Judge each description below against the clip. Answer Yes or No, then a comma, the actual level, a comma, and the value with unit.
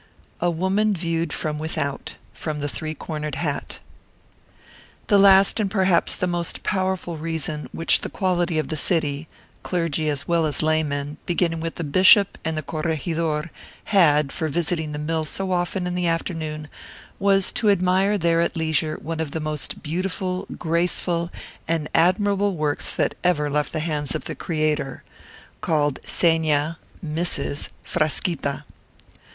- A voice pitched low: No, medium, 165 Hz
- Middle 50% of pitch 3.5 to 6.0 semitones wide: No, average, 2.8 semitones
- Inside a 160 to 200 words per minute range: No, average, 150 wpm